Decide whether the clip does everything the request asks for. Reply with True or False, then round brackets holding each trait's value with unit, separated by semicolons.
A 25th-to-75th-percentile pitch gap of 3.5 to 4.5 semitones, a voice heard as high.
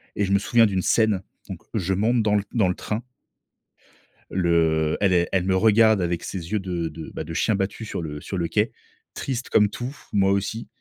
False (3.9 semitones; 95 Hz)